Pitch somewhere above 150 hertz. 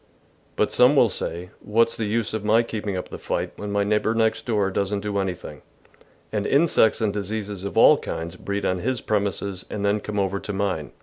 No: low, 105 Hz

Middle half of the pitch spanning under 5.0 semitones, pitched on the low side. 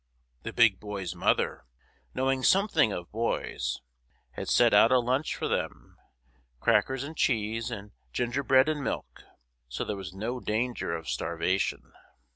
No: average, 5.3 semitones; low, 115 Hz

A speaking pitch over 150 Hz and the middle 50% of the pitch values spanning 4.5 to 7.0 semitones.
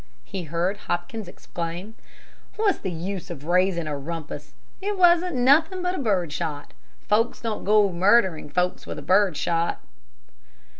Yes: medium, 185 Hz; average, 5.2 semitones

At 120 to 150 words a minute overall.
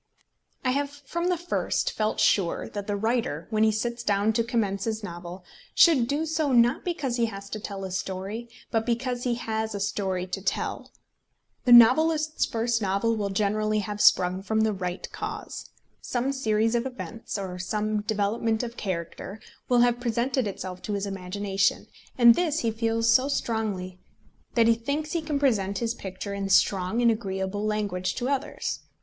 No: average, 180 wpm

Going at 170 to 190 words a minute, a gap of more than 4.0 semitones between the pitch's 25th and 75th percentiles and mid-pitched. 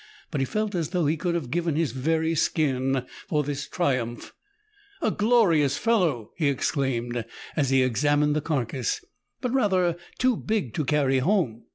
Yes: average, 175 wpm; average, 5.1 semitones; medium, 150 Hz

